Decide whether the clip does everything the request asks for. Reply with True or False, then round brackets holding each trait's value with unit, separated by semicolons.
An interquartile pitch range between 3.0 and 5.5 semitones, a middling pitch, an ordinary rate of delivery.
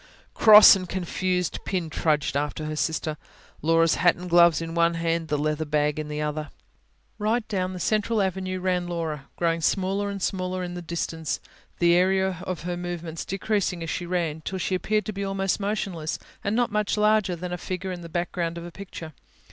False (2.6 semitones; 175 Hz; 195 wpm)